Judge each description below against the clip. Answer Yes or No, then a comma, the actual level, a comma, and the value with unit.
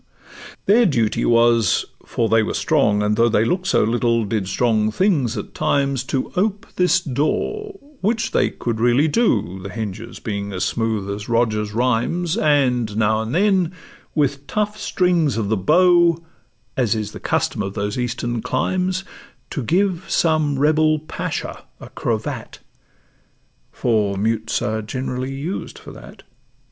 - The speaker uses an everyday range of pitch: No, wide, 7.3 semitones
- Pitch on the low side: Yes, low, 125 Hz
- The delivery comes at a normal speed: Yes, average, 150 wpm